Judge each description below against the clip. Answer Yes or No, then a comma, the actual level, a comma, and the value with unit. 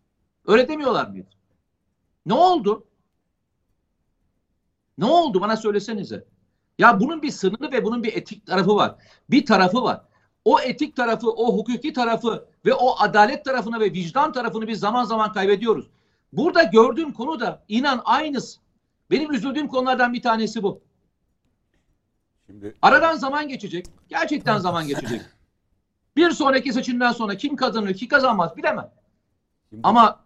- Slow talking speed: No, average, 130 wpm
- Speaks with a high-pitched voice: Yes, high, 225 Hz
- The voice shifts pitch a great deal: Yes, wide, 5.8 semitones